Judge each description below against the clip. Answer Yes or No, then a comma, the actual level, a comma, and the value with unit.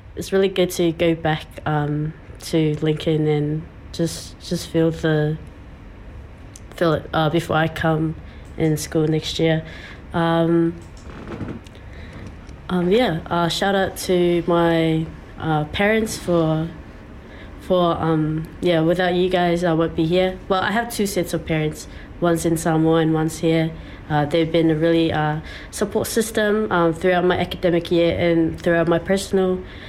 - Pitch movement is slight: Yes, narrow, 2.3 semitones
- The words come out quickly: No, average, 150 wpm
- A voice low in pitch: No, medium, 165 Hz